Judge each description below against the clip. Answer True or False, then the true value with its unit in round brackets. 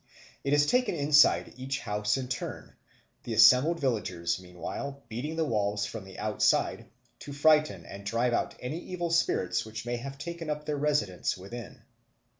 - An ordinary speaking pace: True (165 wpm)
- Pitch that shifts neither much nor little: False (6.3 semitones)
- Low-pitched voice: True (130 Hz)